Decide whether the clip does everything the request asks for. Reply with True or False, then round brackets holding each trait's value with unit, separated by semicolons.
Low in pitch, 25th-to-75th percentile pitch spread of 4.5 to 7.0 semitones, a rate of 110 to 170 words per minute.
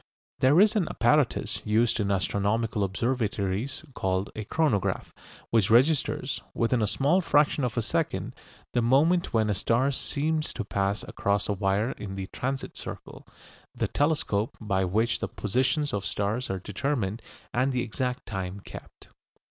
True (115 Hz; 5.0 semitones; 155 wpm)